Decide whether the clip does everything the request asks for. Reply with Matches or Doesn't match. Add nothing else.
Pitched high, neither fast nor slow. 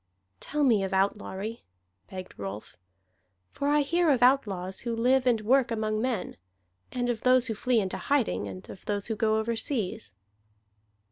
Matches